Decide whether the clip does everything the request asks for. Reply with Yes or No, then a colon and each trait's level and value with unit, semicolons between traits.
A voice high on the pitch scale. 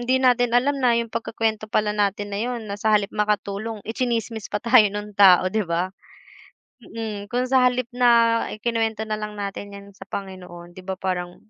Yes: high, 215 Hz